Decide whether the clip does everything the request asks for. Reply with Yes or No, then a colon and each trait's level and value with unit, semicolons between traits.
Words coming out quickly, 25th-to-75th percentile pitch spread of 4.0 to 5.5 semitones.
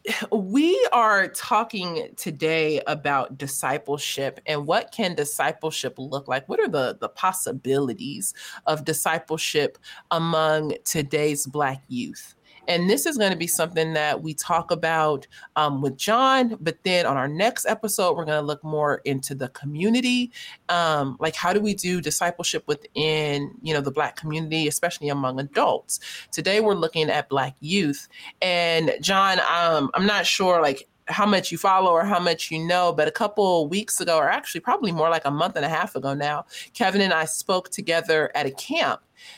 No: average, 175 wpm; average, 4.3 semitones